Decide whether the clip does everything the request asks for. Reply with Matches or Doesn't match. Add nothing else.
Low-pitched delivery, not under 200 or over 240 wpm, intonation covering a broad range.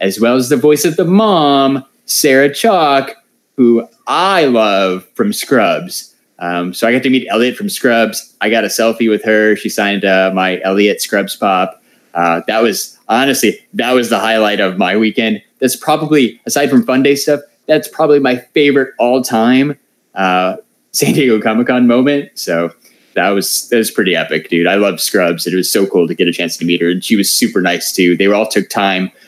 Matches